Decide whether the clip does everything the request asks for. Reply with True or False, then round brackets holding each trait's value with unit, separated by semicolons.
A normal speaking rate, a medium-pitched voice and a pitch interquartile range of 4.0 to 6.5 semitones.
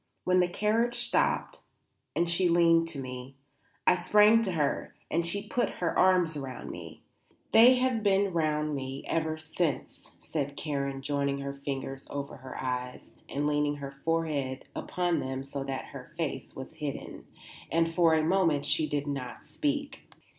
True (160 wpm; 155 Hz; 4.3 semitones)